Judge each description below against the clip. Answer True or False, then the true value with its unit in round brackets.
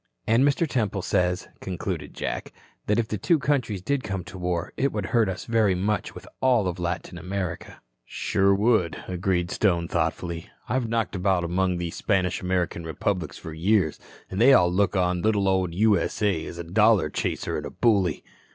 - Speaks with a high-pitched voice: False (95 Hz)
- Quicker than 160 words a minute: True (180 wpm)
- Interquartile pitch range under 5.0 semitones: True (3.6 semitones)